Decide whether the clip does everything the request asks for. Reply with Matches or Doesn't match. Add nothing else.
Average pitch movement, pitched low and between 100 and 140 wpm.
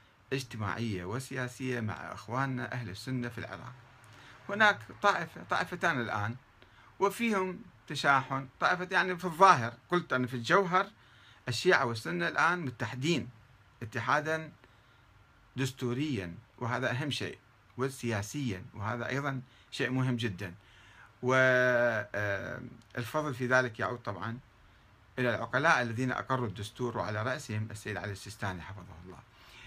Matches